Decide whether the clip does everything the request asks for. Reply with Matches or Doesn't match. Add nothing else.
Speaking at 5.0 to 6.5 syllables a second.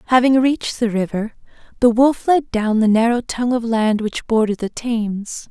Matches